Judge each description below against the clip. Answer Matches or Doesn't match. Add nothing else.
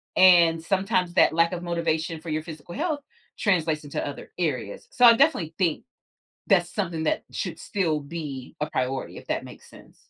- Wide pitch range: Doesn't match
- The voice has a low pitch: Doesn't match